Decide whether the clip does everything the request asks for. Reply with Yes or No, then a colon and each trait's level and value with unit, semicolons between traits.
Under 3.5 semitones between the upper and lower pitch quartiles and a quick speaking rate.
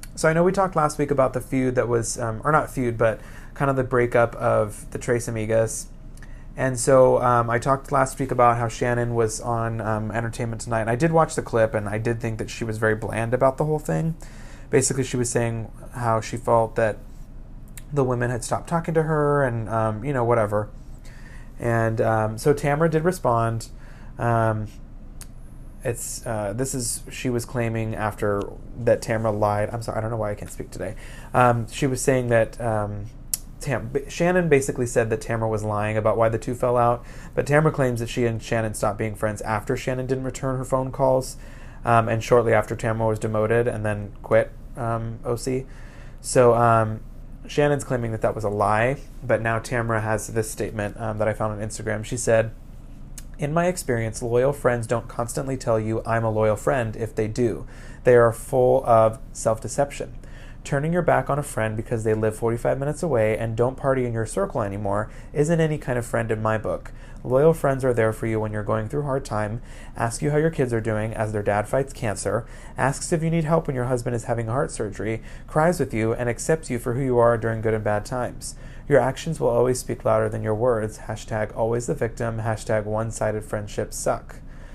Yes: average, 3.0 semitones; fast, 210 wpm